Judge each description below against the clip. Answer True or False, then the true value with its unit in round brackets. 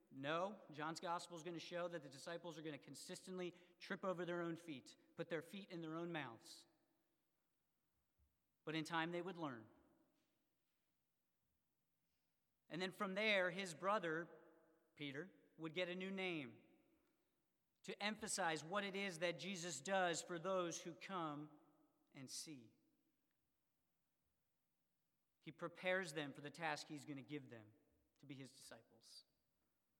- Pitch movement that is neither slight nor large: True (3.2 semitones)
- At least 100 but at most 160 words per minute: True (145 wpm)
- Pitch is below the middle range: False (170 Hz)